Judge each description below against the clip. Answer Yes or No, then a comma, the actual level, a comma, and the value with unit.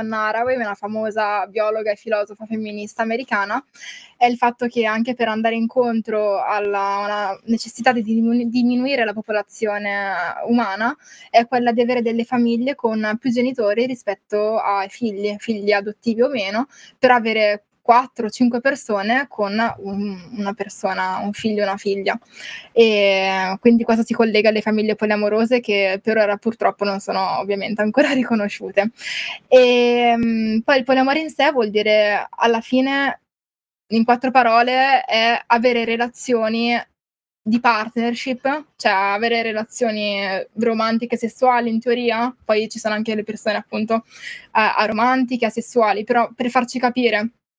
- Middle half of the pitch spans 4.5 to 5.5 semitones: No, narrow, 2.5 semitones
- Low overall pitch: No, high, 225 Hz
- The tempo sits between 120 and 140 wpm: Yes, average, 135 wpm